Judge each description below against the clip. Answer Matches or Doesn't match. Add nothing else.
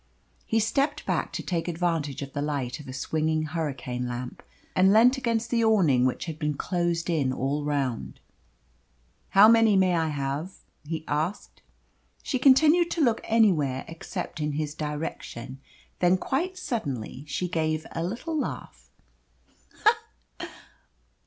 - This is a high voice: Doesn't match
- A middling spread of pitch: Doesn't match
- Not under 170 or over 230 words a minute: Doesn't match